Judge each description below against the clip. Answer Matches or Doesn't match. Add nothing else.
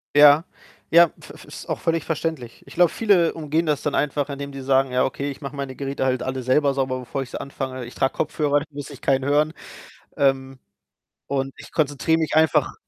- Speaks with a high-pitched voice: Doesn't match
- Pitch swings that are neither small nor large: Doesn't match